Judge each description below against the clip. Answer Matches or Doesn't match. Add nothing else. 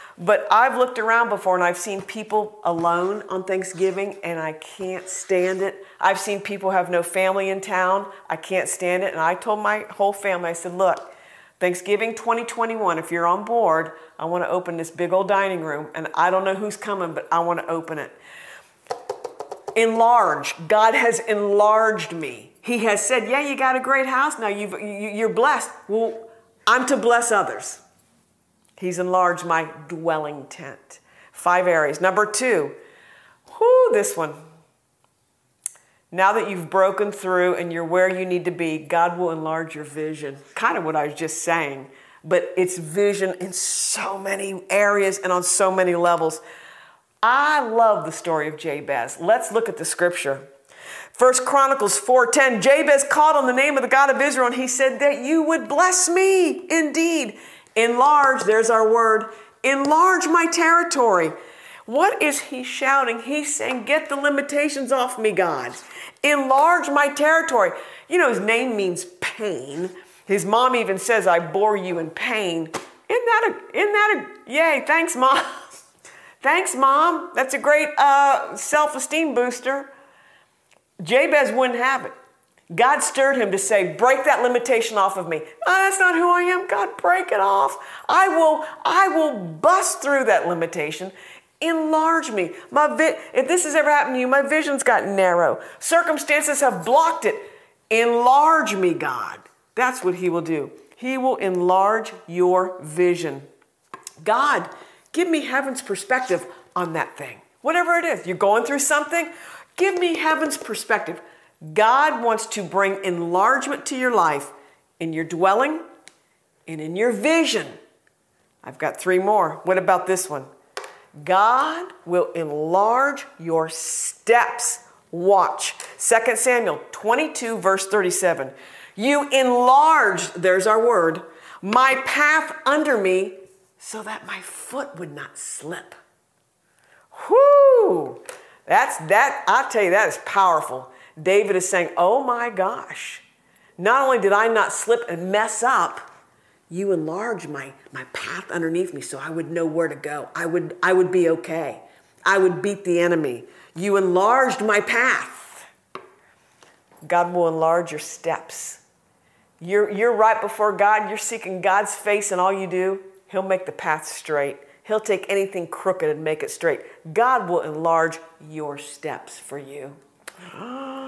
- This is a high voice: Matches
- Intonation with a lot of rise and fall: Matches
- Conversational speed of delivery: Matches